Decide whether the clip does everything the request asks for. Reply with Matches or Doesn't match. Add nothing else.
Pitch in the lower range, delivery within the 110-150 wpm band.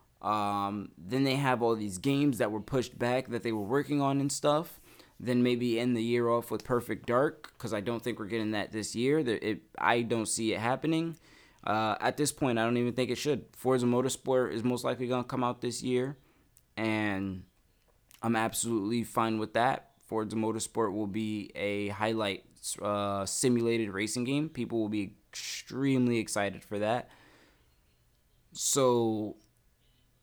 Doesn't match